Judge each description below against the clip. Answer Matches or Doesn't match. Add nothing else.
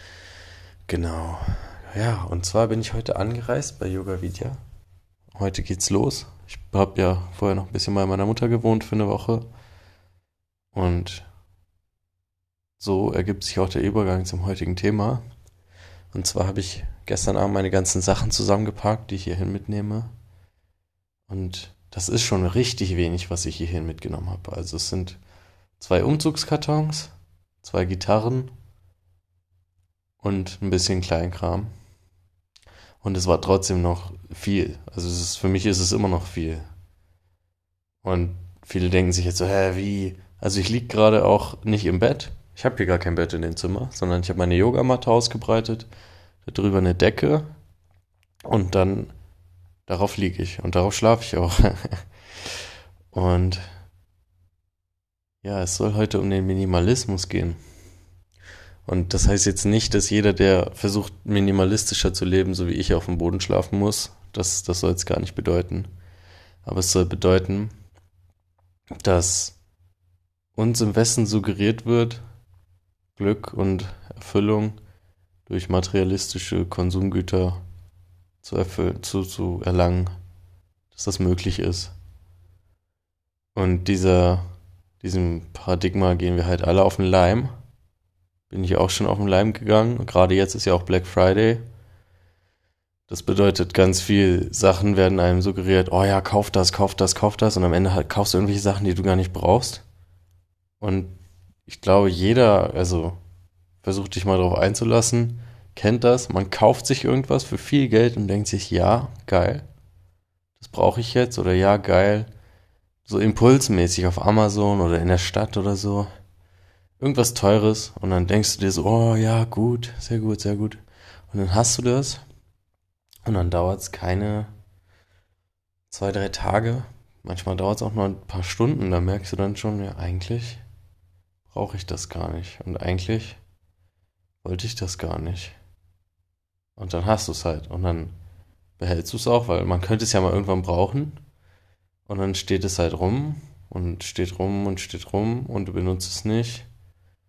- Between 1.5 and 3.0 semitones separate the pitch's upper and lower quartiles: Matches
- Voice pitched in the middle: Doesn't match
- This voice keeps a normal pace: Matches